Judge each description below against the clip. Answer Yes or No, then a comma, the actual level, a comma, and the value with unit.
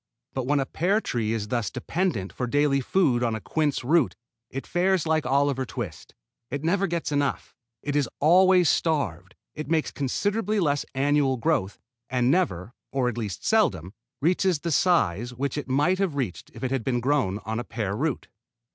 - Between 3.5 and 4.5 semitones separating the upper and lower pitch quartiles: No, average, 5.3 semitones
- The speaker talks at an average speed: Yes, average, 180 wpm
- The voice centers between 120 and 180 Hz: Yes, medium, 140 Hz